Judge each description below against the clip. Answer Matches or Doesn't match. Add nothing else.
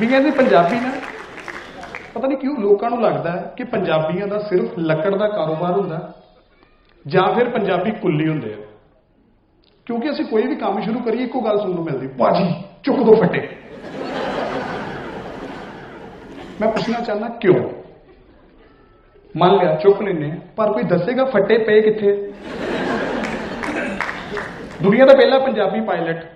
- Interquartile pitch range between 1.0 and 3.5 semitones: Doesn't match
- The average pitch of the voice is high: Matches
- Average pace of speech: Matches